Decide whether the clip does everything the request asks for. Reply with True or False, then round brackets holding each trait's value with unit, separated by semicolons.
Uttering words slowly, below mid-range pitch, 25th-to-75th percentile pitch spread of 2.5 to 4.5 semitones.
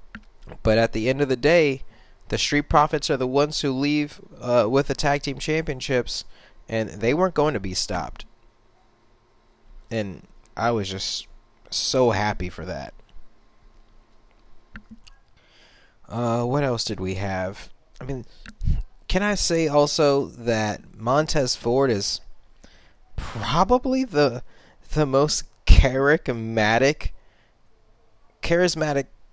False (120 wpm; 125 Hz; 5.0 semitones)